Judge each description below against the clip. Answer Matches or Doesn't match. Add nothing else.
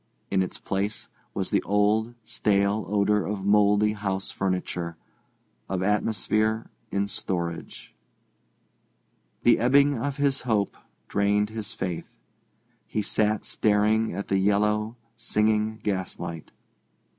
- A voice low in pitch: Matches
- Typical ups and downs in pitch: Doesn't match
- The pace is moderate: Doesn't match